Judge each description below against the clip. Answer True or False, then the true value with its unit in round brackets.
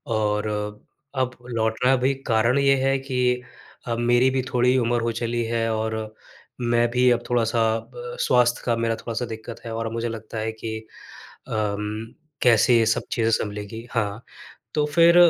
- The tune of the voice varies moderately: False (1.8 semitones)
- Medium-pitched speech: False (115 Hz)